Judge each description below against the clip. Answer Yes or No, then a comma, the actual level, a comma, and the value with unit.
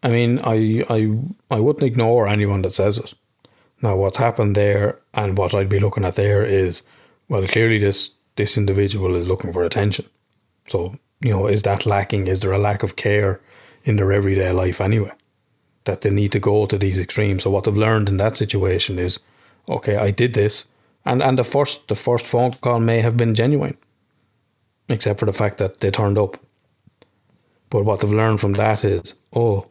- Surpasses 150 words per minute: Yes, average, 195 wpm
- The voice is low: Yes, low, 105 Hz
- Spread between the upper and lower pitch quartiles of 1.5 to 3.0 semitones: Yes, narrow, 2.5 semitones